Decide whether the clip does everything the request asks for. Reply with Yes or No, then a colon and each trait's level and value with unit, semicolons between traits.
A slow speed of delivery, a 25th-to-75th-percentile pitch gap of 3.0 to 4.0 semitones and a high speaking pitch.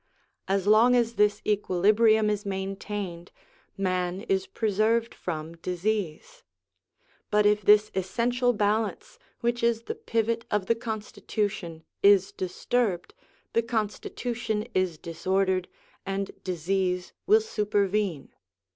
Yes: slow, 110 wpm; average, 3.4 semitones; high, 210 Hz